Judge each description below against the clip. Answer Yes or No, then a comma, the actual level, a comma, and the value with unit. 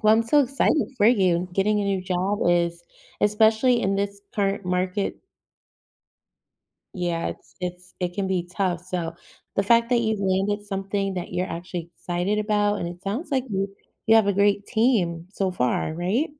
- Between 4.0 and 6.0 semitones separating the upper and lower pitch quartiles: No, average, 2.8 semitones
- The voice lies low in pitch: No, high, 195 Hz